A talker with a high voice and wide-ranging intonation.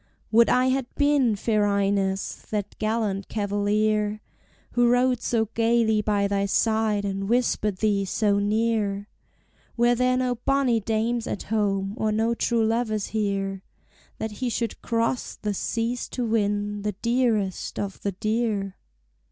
No: high, 215 Hz; narrow, 2.5 semitones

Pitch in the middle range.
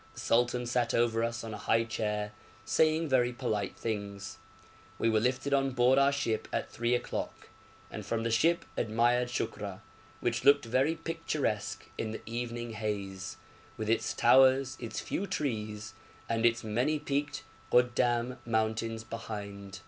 No: low, 120 Hz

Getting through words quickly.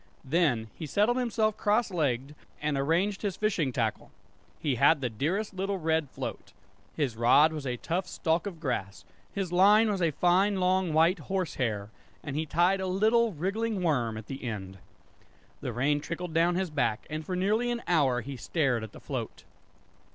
No: average, 180 wpm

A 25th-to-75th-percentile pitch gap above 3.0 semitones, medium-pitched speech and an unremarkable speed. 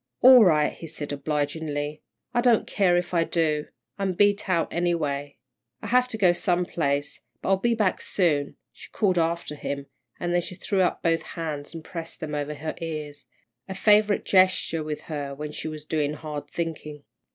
Yes: average, 3.8 semitones; medium, 165 Hz; average, 185 wpm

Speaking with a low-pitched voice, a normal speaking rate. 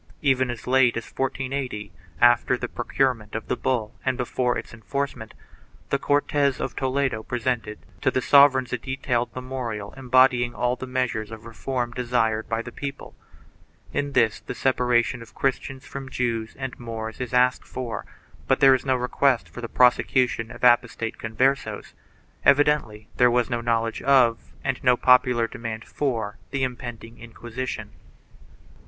Yes: low, 125 Hz; average, 160 wpm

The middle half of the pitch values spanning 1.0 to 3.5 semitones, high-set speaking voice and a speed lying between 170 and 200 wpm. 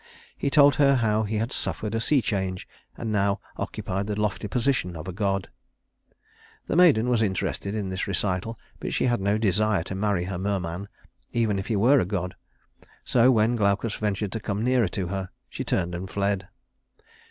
No: average, 2.9 semitones; low, 105 Hz; average, 185 wpm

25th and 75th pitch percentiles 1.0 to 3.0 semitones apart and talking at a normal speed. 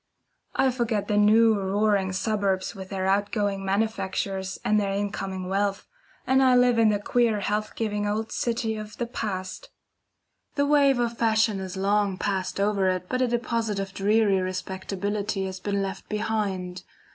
Yes: narrow, 2.4 semitones; average, 165 wpm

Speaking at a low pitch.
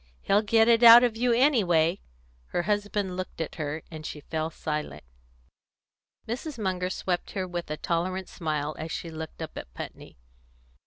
No: medium, 180 Hz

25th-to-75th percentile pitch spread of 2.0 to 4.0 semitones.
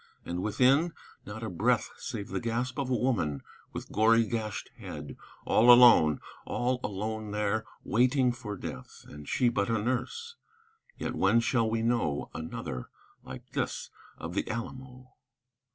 Yes: average, 3.5 semitones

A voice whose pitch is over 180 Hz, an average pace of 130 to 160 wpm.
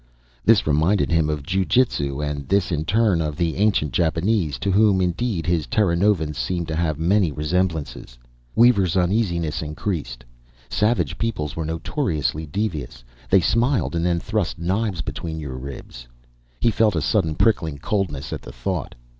No: very low, 85 Hz; average, 155 wpm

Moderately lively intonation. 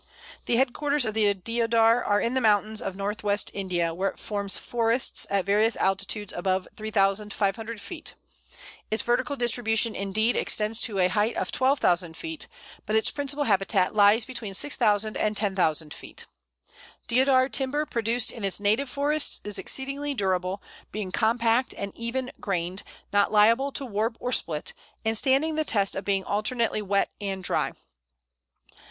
Yes: average, 3.7 semitones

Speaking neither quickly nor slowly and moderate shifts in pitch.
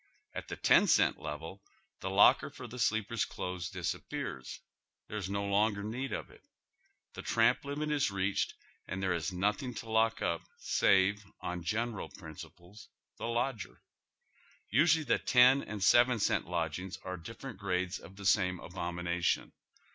Yes: average, 155 wpm; average, 4.4 semitones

